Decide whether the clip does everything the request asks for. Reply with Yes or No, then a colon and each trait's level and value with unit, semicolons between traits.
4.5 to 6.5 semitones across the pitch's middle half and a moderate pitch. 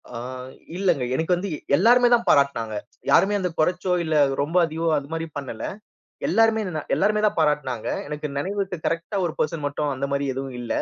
Yes: average, 4.9 semitones; medium, 160 Hz